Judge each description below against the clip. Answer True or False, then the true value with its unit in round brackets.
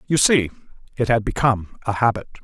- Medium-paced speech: True (175 wpm)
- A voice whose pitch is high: False (115 Hz)